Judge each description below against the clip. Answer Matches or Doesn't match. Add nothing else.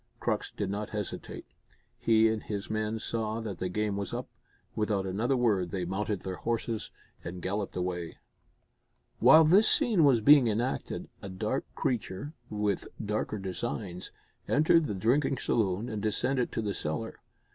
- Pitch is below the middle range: Matches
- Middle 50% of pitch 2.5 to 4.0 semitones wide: Matches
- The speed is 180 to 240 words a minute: Doesn't match